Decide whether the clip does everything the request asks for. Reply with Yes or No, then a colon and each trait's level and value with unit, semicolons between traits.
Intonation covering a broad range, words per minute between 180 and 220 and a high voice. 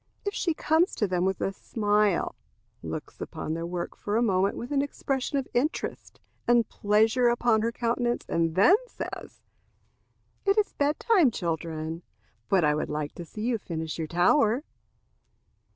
No: wide, 6.7 semitones; average, 160 wpm; high, 215 Hz